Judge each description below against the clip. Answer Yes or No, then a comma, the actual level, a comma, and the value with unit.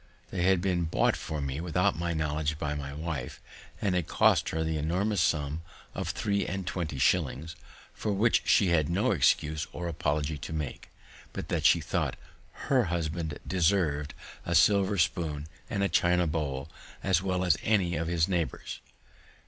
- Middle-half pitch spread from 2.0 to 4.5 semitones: Yes, average, 3.3 semitones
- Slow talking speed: No, average, 170 wpm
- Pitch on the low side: Yes, very low, 85 Hz